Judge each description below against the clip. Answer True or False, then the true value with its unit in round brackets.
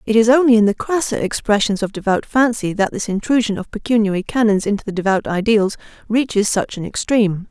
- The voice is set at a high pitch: True (215 Hz)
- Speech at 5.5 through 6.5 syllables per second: True (5.9 syllables/s)